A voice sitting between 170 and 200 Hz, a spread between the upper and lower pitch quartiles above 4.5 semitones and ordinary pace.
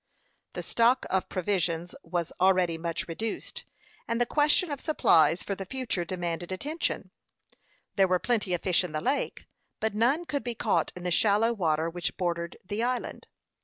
Yes: high, 190 Hz; wide, 5.5 semitones; average, 170 wpm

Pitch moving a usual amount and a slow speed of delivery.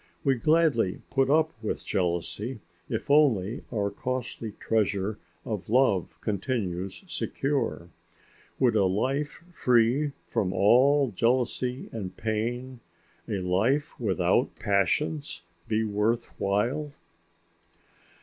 Yes: average, 4.9 semitones; slow, 100 wpm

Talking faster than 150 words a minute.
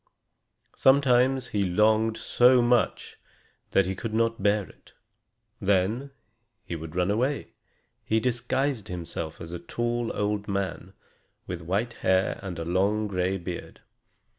No: slow, 135 wpm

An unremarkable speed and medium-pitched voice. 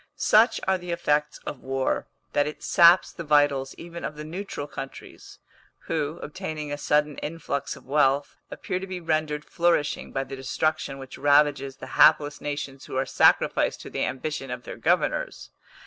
Yes: average, 170 wpm; medium, 150 Hz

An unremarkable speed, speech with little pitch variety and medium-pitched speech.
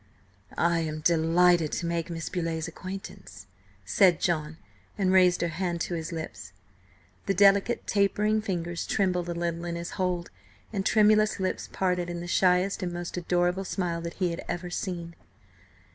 Yes: average, 160 wpm; narrow, 1.9 semitones; medium, 175 Hz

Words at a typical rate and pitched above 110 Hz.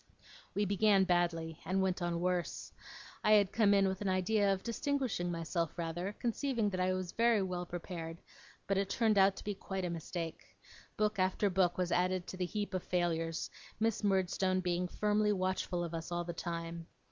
Yes: average, 190 wpm; medium, 185 Hz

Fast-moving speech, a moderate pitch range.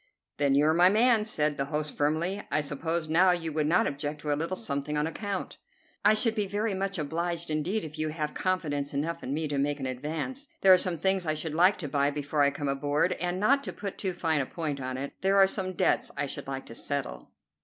Yes: fast, 240 wpm; average, 4.3 semitones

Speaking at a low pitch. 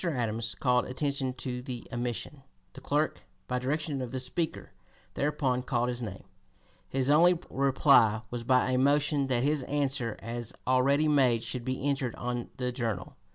Yes: low, 130 Hz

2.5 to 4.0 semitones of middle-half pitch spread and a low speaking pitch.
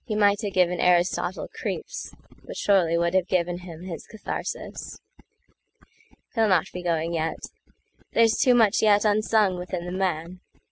No: average, 3.2 semitones; medium, 185 Hz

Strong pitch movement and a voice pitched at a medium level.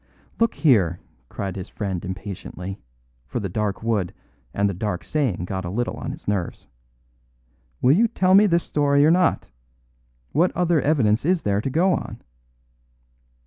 No: wide, 8.9 semitones; low, 110 Hz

